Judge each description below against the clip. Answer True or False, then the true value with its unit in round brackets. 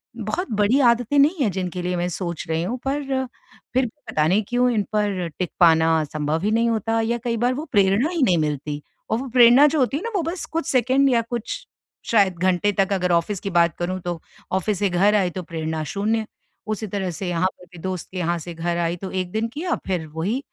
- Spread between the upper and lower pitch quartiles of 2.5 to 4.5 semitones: False (5.3 semitones)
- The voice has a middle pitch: False (195 Hz)